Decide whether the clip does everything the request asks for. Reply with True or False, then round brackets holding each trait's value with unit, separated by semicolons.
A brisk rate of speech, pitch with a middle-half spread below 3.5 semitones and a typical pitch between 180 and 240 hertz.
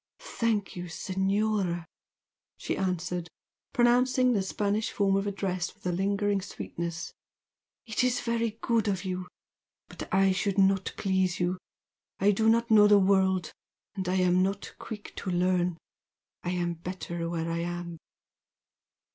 False (145 wpm; 2.7 semitones; 190 Hz)